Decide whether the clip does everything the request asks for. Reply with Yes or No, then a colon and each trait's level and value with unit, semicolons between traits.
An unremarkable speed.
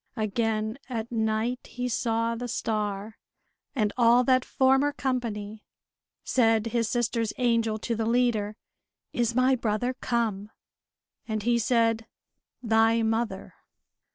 No: slow, 120 wpm